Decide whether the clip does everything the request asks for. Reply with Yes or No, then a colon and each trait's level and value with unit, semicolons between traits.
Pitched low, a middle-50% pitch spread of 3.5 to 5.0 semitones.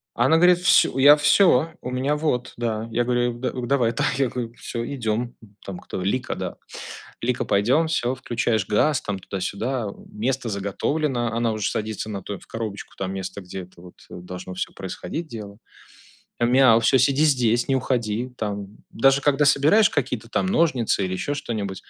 Yes: low, 120 Hz; average, 4.7 semitones